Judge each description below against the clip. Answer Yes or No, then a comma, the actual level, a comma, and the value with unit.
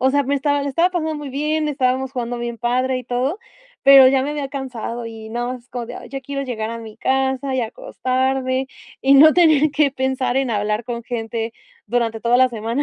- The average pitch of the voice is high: Yes, very high, 260 Hz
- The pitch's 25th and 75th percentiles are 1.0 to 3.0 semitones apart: Yes, narrow, 2.5 semitones